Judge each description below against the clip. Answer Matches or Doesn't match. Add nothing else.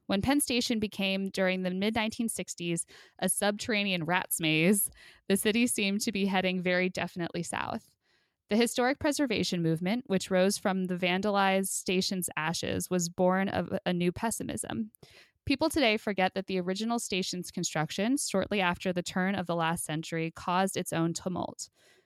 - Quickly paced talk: Doesn't match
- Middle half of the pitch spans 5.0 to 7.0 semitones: Doesn't match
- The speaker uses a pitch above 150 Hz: Matches